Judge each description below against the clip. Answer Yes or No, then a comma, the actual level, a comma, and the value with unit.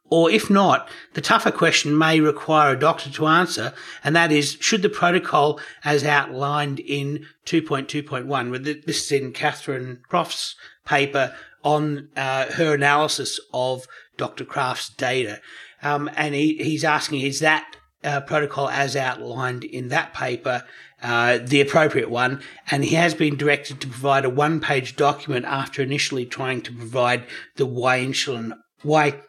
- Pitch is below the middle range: No, medium, 145 Hz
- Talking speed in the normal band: Yes, average, 150 wpm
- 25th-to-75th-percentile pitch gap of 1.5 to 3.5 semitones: Yes, narrow, 2.6 semitones